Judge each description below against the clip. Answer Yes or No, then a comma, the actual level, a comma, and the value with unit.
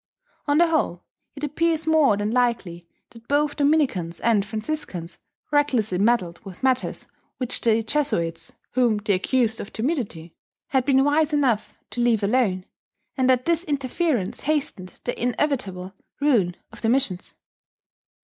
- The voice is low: No, high, 245 Hz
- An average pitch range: No, wide, 6.4 semitones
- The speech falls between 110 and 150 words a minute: Yes, average, 140 wpm